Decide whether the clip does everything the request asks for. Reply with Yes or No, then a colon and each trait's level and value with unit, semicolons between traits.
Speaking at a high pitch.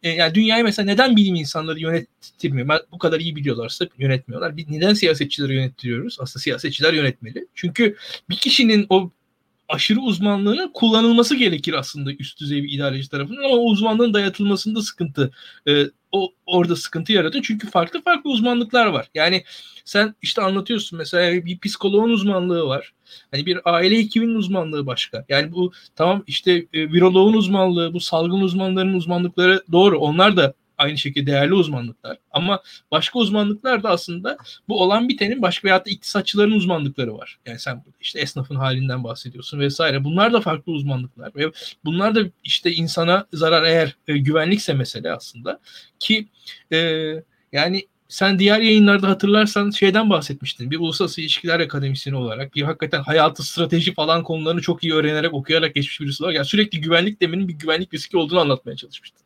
No: medium, 175 Hz